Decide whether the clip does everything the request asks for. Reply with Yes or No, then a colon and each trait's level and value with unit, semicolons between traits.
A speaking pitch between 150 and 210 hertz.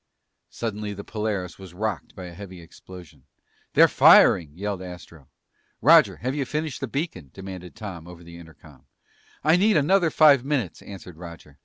No: very low, 95 Hz